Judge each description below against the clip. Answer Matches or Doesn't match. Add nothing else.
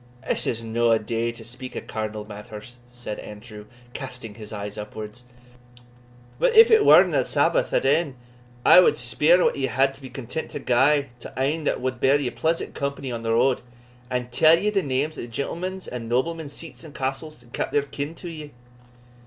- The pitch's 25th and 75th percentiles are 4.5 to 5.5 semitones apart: Matches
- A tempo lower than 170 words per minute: Doesn't match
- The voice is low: Matches